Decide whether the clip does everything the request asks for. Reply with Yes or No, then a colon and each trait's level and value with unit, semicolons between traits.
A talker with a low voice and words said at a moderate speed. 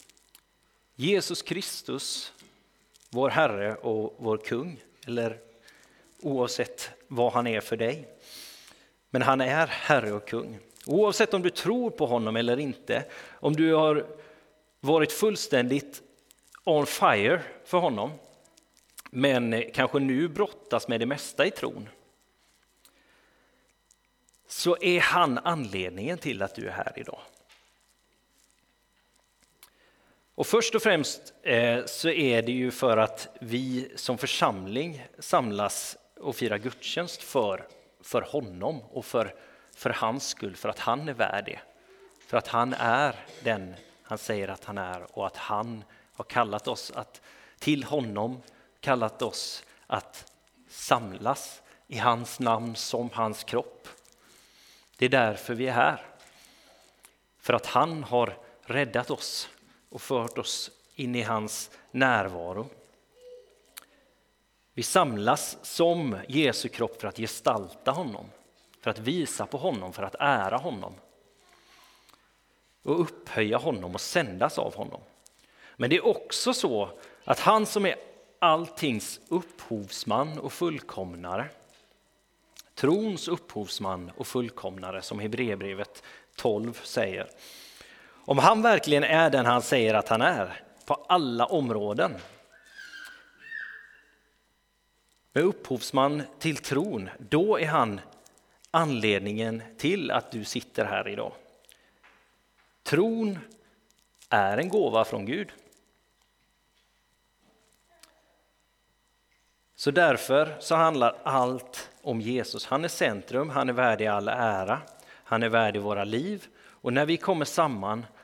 No: low, 125 Hz; slow, 120 wpm